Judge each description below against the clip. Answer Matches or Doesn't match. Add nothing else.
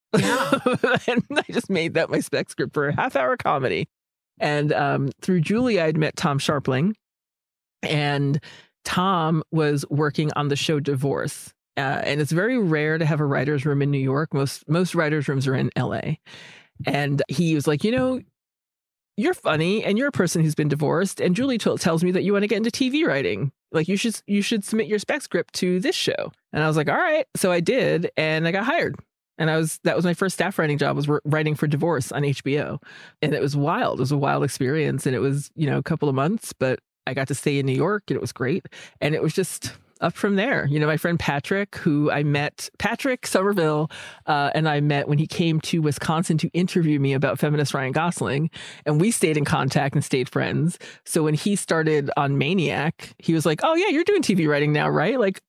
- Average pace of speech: Doesn't match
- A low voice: Doesn't match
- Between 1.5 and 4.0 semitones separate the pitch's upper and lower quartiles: Doesn't match